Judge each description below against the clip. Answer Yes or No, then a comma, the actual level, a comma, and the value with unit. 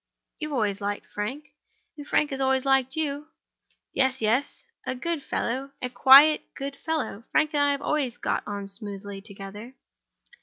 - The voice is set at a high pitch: Yes, very high, 265 Hz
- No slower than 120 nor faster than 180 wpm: Yes, average, 150 wpm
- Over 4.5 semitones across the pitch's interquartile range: Yes, average, 5.3 semitones